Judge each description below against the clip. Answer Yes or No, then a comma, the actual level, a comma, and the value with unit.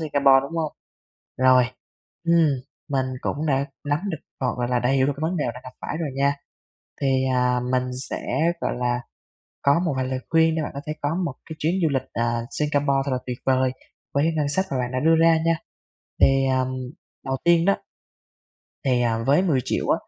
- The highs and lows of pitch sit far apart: No, average, 3.4 semitones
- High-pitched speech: No, medium, 140 Hz